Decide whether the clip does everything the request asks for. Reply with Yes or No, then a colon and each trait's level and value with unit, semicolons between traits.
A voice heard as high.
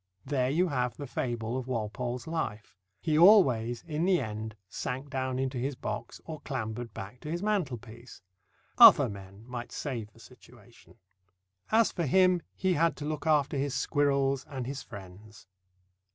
No: low, 130 Hz